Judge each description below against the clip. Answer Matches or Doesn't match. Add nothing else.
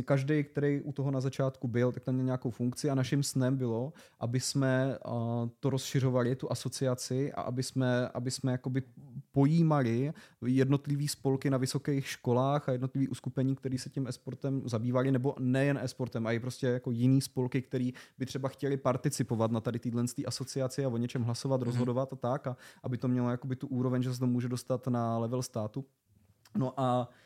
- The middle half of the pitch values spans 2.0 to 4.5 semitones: Doesn't match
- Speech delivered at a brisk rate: Matches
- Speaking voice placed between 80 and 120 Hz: Doesn't match